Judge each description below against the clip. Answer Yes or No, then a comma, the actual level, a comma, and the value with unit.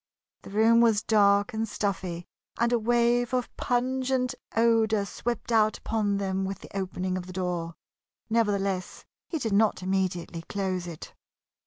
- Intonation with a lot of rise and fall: No, average, 3.6 semitones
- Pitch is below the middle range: No, high, 205 Hz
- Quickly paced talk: No, average, 150 wpm